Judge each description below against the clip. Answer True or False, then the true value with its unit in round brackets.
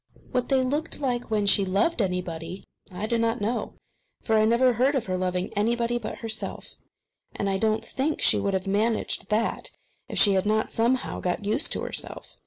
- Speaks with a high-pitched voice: True (220 Hz)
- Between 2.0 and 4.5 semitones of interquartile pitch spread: True (3.6 semitones)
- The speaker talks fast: False (195 wpm)